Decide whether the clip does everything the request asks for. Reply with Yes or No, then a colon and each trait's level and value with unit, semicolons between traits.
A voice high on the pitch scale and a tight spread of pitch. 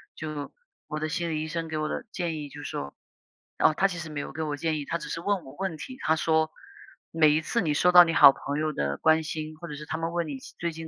No: medium, 160 Hz; narrow, 1.7 semitones